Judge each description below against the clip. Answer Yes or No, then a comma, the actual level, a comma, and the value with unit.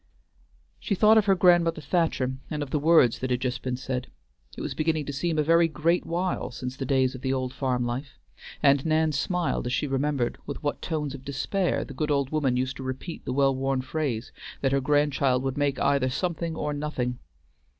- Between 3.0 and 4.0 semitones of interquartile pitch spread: Yes, average, 3.3 semitones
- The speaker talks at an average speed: No, fast, 210 wpm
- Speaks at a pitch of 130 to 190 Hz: Yes, medium, 140 Hz